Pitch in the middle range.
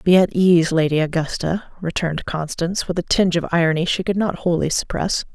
Yes: medium, 170 Hz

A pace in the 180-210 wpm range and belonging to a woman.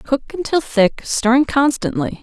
No: slow, 135 wpm; female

